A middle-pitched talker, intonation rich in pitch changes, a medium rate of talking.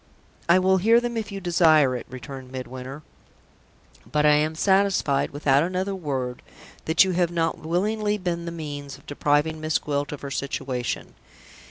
No: medium, 155 Hz; average, 4.7 semitones; average, 165 wpm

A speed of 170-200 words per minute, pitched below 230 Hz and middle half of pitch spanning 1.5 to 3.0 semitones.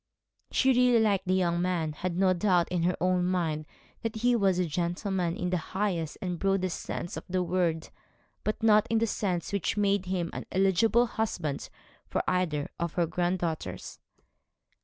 Yes: average, 175 wpm; medium, 185 Hz; average, 2.7 semitones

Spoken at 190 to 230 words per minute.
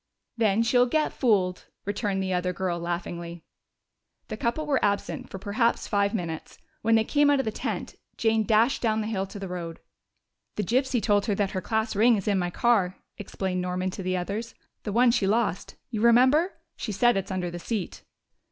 Yes: average, 200 wpm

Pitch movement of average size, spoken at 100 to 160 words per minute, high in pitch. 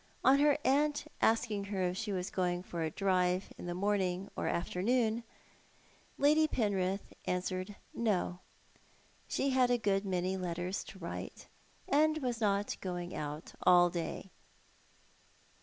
Yes: average, 4.4 semitones; average, 140 wpm; high, 195 Hz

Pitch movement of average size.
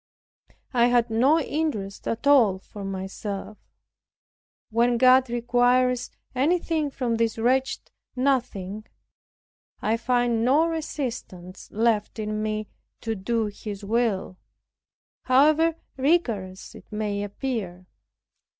Yes: average, 3.7 semitones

